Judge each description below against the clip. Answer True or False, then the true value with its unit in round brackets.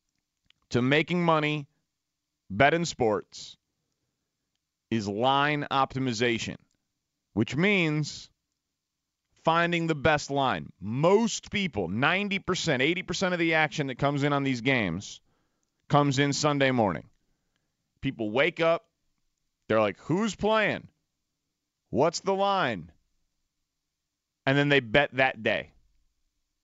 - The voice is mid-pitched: True (145 Hz)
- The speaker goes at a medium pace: False (105 wpm)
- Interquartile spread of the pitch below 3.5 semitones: False (5.1 semitones)